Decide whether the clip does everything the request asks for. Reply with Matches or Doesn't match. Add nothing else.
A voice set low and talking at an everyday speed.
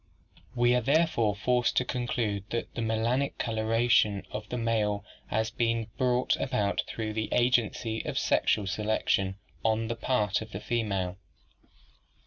Matches